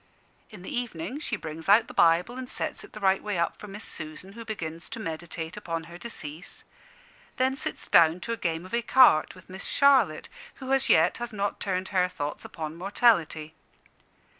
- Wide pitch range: Yes, wide, 5.9 semitones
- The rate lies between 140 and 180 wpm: No, average, 190 wpm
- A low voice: No, medium, 185 Hz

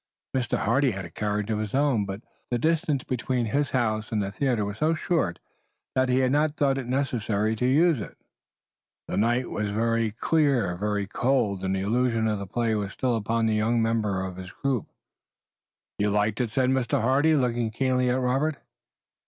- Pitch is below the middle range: Yes, low, 120 Hz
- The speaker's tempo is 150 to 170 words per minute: No, average, 190 wpm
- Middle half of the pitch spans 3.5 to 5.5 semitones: Yes, average, 3.9 semitones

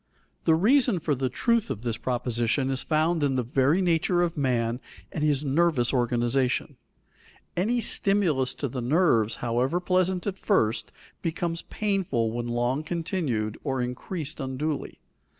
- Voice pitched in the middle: Yes, medium, 145 Hz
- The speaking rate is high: No, average, 145 wpm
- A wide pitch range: Yes, wide, 6.0 semitones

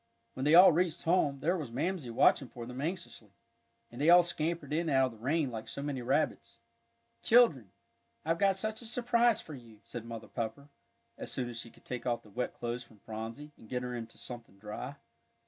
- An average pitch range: No, wide, 6.1 semitones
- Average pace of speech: No, fast, 210 wpm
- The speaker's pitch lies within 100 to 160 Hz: Yes, low, 135 Hz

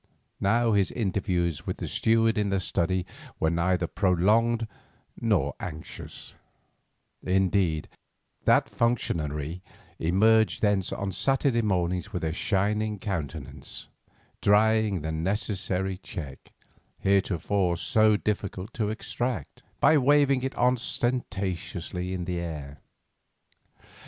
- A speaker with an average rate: No, slow, 105 wpm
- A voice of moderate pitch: No, very low, 95 Hz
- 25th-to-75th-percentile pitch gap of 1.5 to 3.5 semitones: No, average, 3.9 semitones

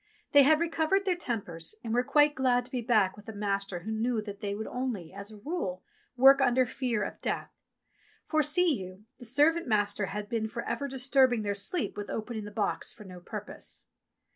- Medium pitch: No, high, 230 Hz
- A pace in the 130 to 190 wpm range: No, fast, 205 wpm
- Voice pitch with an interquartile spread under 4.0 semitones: No, average, 4.8 semitones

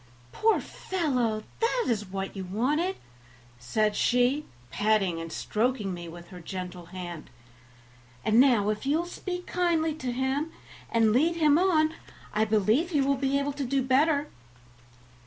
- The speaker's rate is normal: Yes, average, 155 wpm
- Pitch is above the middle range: Yes, very high, 255 Hz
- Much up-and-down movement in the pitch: Yes, wide, 6.8 semitones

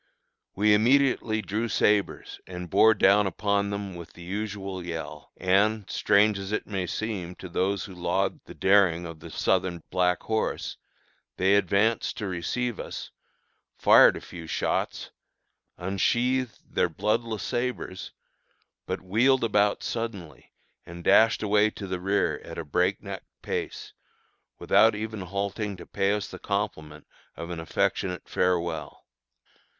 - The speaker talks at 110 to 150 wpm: Yes, average, 140 wpm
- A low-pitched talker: Yes, low, 100 Hz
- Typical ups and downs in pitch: Yes, average, 3.1 semitones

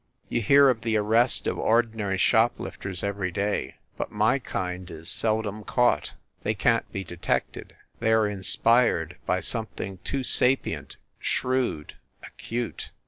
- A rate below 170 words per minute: Yes, average, 140 wpm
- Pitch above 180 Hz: No, low, 110 Hz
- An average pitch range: Yes, average, 3.8 semitones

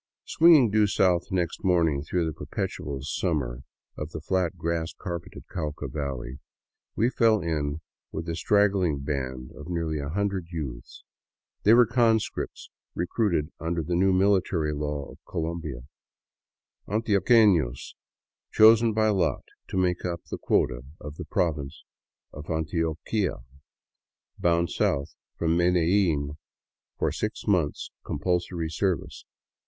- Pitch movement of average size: Yes, average, 4.3 semitones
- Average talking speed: No, slow, 125 wpm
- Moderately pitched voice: No, very low, 85 Hz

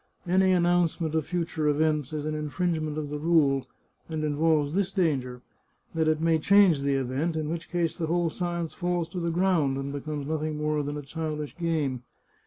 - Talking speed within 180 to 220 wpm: Yes, average, 195 wpm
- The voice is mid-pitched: Yes, medium, 155 Hz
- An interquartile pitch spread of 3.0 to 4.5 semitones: No, narrow, 2.5 semitones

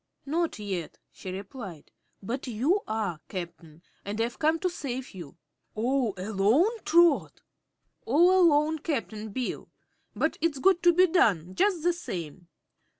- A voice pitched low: No, very high, 250 Hz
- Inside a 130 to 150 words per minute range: Yes, average, 140 wpm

